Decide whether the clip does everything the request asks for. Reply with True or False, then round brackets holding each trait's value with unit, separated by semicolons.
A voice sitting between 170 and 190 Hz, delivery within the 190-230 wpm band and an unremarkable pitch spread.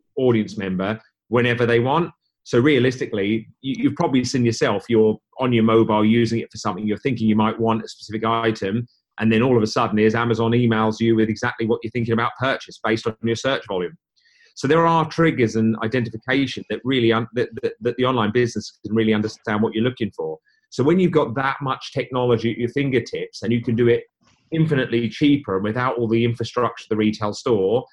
False (115 Hz; 205 wpm; 3.0 semitones)